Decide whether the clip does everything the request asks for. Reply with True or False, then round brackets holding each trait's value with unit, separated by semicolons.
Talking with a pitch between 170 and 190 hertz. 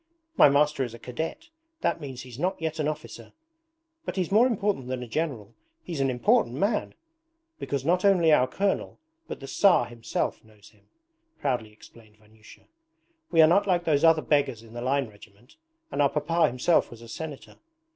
False (140 Hz)